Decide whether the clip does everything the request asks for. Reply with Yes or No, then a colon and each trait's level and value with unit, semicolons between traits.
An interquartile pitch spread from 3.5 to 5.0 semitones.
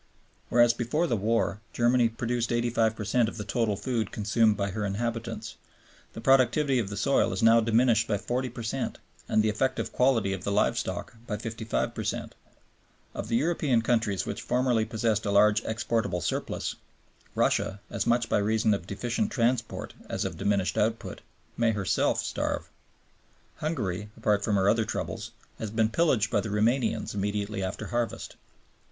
No: narrow, 2.4 semitones